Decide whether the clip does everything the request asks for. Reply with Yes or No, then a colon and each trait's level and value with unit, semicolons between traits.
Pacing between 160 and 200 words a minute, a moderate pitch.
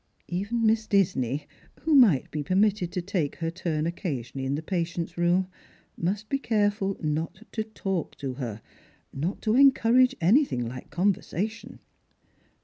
No: average, 145 wpm; medium, 180 Hz